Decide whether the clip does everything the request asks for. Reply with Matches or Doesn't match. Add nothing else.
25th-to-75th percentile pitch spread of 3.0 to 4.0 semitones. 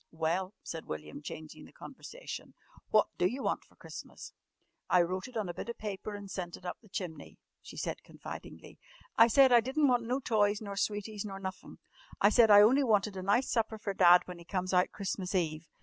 Matches